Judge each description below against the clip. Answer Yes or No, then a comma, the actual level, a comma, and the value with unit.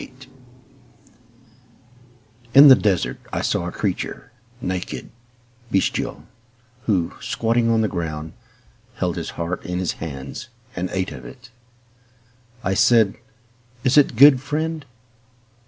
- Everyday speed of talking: No, slow, 120 wpm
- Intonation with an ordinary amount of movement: No, wide, 6.1 semitones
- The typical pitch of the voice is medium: No, low, 110 Hz